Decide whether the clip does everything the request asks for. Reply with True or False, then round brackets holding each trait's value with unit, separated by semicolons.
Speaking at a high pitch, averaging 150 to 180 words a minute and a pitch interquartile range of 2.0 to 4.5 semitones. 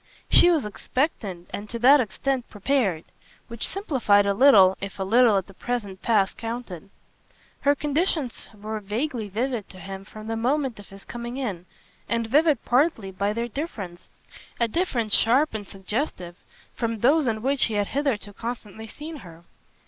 False (225 Hz; 165 wpm; 4.9 semitones)